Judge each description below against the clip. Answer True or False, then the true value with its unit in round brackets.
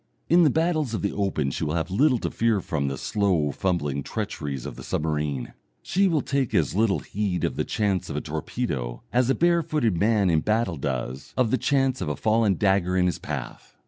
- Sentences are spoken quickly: True (210 wpm)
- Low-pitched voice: True (100 Hz)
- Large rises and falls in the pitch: True (8.1 semitones)